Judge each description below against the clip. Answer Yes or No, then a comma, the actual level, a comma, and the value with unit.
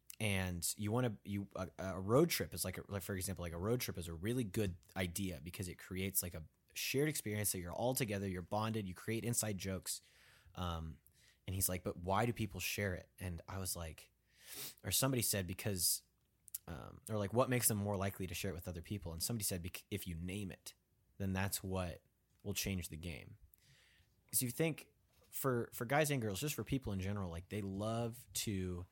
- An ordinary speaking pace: No, fast, 215 wpm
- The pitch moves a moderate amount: Yes, average, 3.5 semitones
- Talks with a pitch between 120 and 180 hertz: No, low, 100 Hz